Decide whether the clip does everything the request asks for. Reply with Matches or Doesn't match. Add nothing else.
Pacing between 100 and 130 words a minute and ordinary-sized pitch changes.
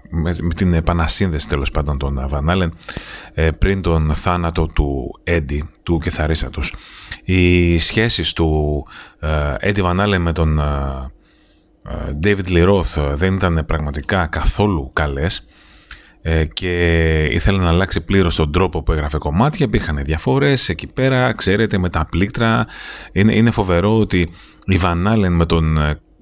Matches